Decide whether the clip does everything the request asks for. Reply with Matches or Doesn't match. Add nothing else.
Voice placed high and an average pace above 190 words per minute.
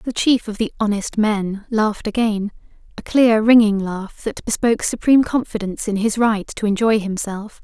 Doesn't match